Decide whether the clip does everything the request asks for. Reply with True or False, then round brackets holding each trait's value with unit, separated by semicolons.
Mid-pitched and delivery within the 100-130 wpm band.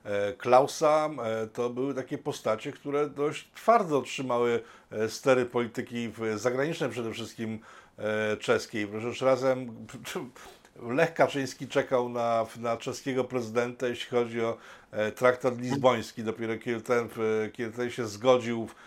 False (120 Hz; 120 wpm)